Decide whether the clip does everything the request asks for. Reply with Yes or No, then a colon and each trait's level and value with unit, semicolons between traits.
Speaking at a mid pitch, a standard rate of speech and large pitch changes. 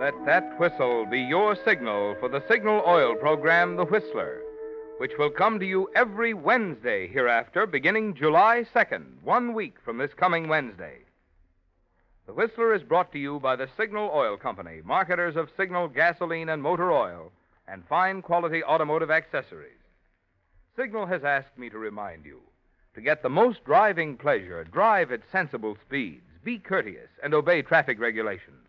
Yes: medium, 170 Hz; average, 160 wpm; wide, 7.6 semitones